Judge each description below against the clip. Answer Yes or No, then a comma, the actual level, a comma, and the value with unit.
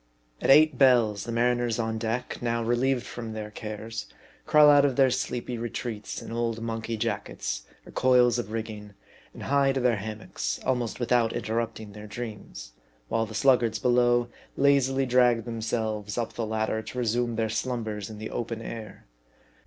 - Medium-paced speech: Yes, average, 170 wpm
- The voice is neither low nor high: No, low, 115 Hz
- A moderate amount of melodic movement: No, narrow, 2.1 semitones